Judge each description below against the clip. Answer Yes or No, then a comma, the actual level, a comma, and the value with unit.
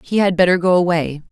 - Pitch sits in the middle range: Yes, medium, 175 Hz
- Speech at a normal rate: No, fast, 230 wpm